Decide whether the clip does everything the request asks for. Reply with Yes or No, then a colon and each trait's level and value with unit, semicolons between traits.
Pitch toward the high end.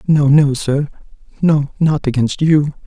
No: medium, 145 Hz